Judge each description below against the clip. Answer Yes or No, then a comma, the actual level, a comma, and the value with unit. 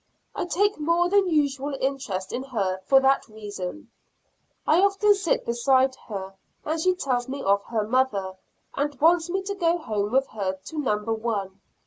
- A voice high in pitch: Yes, very high, 265 Hz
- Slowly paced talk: No, average, 170 wpm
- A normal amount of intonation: No, wide, 7.9 semitones